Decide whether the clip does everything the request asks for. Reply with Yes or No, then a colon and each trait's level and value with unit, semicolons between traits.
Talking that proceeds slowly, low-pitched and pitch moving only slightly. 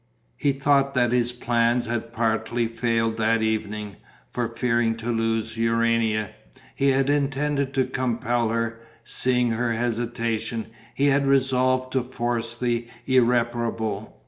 Yes: slow, 130 wpm; low, 120 Hz; narrow, 2.0 semitones